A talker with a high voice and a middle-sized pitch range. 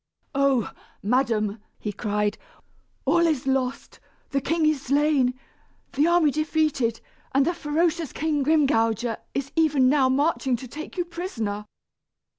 Yes: very high, 275 Hz; average, 4.1 semitones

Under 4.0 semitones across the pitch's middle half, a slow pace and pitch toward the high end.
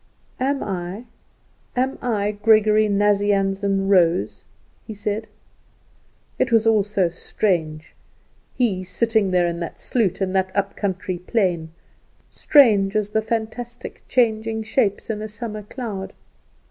Yes: narrow, 2.5 semitones; slow, 120 wpm; high, 205 Hz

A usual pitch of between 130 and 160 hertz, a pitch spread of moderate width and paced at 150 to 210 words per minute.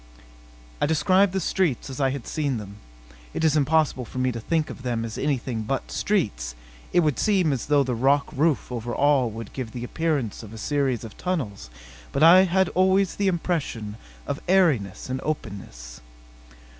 No: medium, 140 Hz; wide, 6.1 semitones; average, 180 wpm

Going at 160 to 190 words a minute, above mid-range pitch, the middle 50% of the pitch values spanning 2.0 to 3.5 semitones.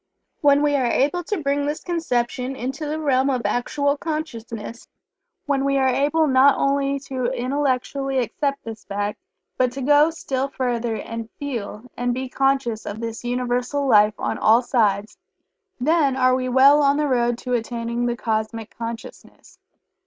Yes: average, 165 wpm; very high, 255 Hz; average, 3.1 semitones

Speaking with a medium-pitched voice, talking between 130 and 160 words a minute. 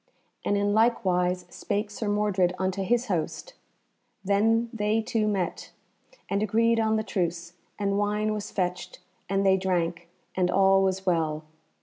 No: high, 200 Hz; average, 150 wpm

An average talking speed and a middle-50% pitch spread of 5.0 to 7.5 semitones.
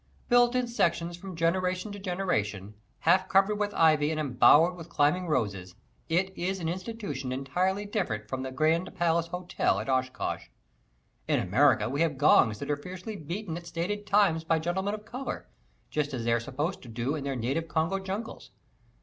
Yes: average, 180 wpm; average, 5.3 semitones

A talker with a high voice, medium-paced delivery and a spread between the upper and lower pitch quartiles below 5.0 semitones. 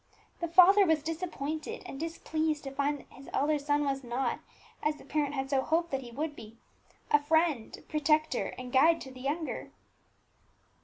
Yes: very high, 295 Hz; average, 175 wpm; average, 2.8 semitones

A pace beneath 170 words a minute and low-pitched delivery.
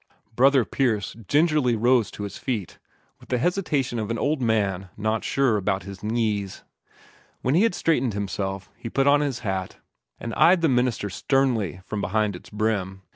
No: average, 175 wpm; low, 115 Hz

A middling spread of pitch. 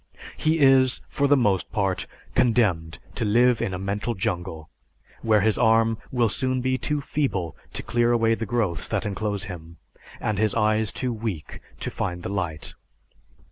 Yes: average, 4.1 semitones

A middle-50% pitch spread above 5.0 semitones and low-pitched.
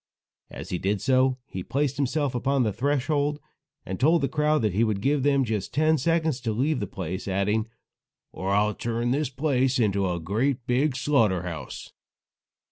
Yes: wide, 5.5 semitones; low, 125 Hz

